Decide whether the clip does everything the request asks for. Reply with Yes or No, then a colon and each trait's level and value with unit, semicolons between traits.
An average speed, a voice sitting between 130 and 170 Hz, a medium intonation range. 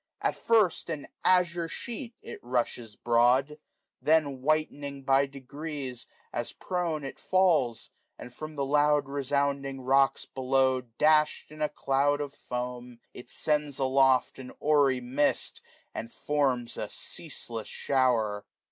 No: slow, 130 wpm; medium, 140 Hz; average, 3.0 semitones